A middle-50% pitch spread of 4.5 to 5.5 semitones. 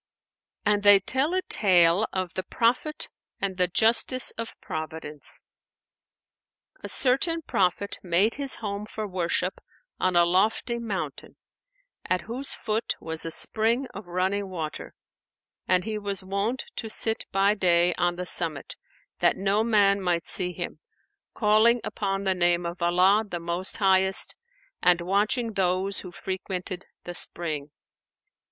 No: average, 3.5 semitones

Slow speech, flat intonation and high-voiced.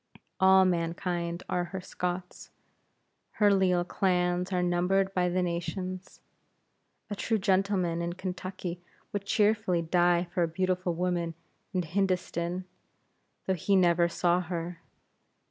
No: slow, 125 wpm; narrow, 1.4 semitones; medium, 180 Hz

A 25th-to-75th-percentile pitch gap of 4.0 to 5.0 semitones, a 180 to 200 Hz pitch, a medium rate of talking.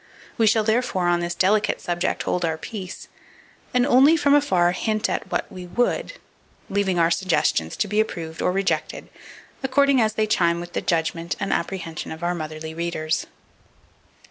Yes: average, 4.3 semitones; medium, 185 Hz; average, 170 wpm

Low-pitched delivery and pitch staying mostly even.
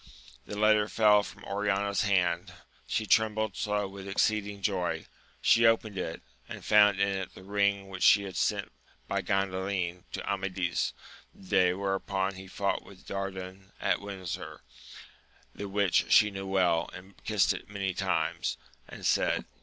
Yes: low, 100 Hz; narrow, 1.4 semitones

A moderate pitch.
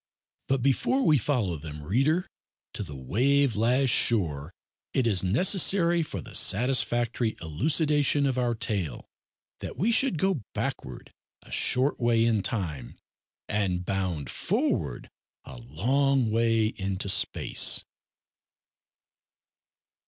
No: low, 115 Hz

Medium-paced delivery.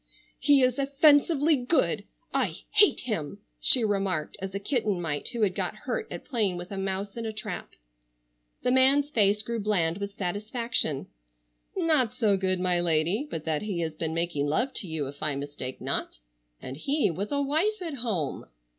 Yes: average, 180 wpm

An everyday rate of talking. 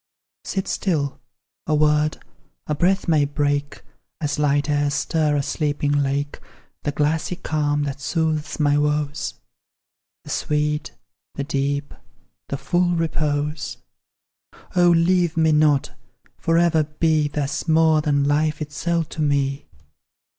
No: slow, 125 wpm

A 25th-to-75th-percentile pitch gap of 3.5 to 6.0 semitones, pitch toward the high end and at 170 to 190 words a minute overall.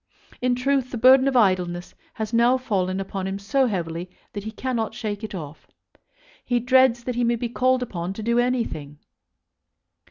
Yes: average, 4.6 semitones; high, 230 Hz; average, 180 wpm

